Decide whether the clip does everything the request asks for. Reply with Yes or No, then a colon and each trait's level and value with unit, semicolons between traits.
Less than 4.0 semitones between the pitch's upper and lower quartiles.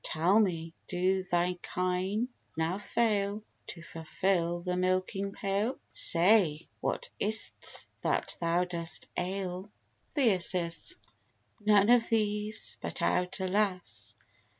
Yes: average, 2.8 semitones